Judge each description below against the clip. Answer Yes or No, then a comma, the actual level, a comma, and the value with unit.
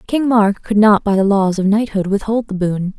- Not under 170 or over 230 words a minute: No, fast, 240 wpm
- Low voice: No, high, 205 Hz